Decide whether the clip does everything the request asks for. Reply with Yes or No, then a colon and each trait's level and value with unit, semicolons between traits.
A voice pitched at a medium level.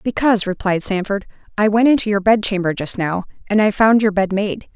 No: high, 205 Hz